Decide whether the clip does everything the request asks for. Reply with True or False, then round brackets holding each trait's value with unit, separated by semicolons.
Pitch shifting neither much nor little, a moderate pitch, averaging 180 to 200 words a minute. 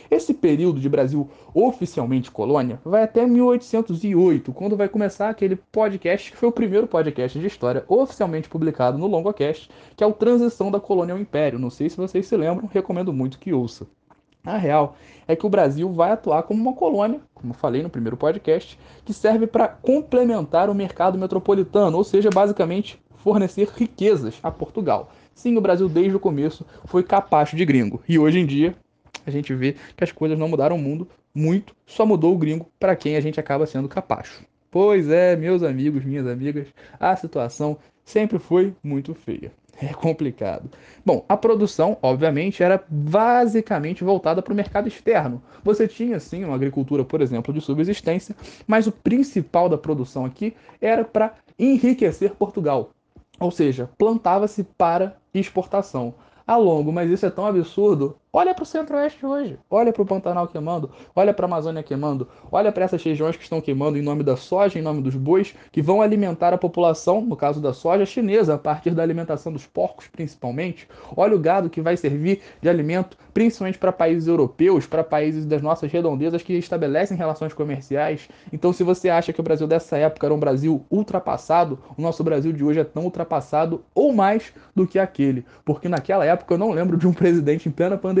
True (4.9 semitones; 175 Hz; 185 wpm)